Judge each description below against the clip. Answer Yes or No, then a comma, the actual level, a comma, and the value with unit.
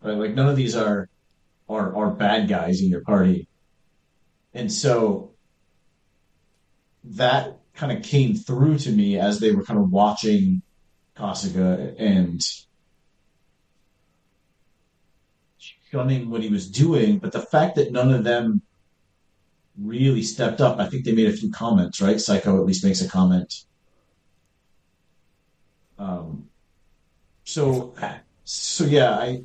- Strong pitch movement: Yes, wide, 6.9 semitones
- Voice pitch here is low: Yes, low, 110 Hz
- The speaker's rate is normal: No, slow, 130 wpm